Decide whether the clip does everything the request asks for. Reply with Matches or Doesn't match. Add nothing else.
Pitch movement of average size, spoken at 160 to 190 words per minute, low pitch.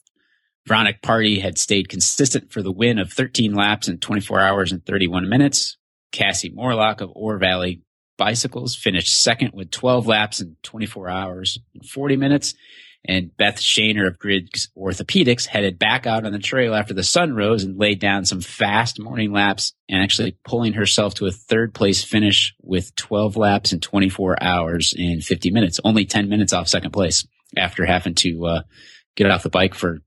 Matches